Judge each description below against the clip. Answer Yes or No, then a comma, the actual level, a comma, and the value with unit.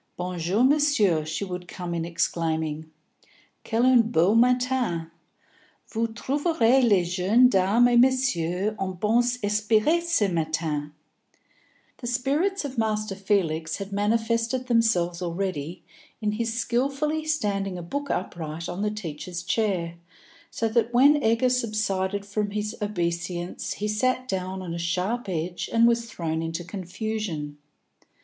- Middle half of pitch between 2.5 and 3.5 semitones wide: No, average, 5.3 semitones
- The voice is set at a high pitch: Yes, high, 205 Hz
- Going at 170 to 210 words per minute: No, slow, 135 wpm